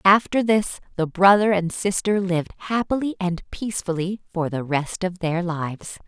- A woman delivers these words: Yes, female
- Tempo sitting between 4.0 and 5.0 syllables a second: Yes, 4.8 syllables/s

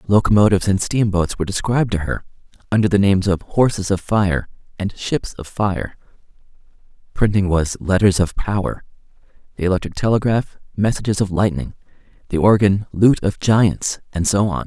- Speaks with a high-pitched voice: No, low, 100 Hz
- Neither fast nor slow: Yes, average, 150 wpm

